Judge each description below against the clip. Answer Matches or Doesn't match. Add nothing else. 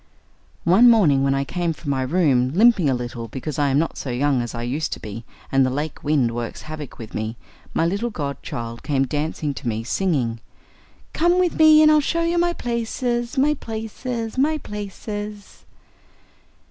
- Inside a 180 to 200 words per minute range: Matches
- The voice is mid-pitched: Matches